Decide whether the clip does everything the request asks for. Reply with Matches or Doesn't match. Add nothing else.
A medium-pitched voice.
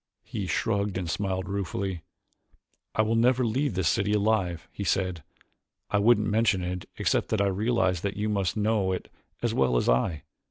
Doesn't match